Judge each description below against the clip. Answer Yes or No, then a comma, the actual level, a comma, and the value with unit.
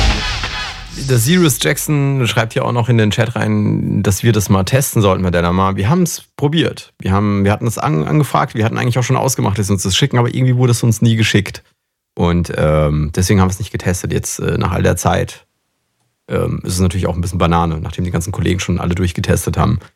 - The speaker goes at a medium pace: No, fast, 225 wpm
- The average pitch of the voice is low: Yes, low, 105 Hz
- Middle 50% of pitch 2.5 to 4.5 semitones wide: No, average, 5.2 semitones